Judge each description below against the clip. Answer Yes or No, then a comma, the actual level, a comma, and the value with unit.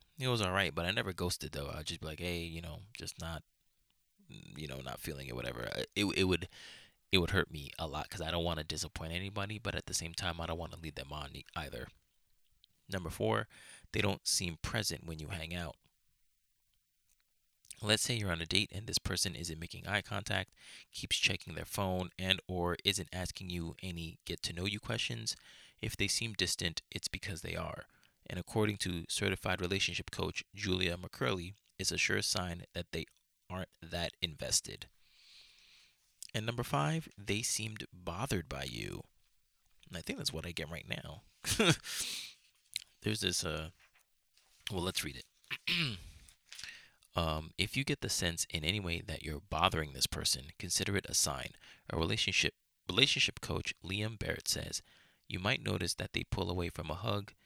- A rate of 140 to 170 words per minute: No, average, 180 wpm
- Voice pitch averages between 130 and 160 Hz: No, very low, 90 Hz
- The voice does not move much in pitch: No, average, 3.6 semitones